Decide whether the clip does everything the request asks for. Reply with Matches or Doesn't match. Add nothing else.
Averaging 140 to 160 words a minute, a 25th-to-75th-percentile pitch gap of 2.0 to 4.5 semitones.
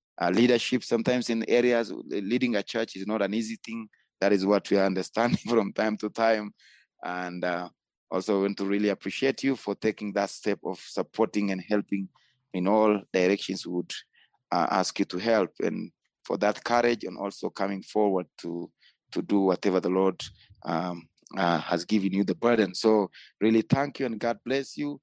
Doesn't match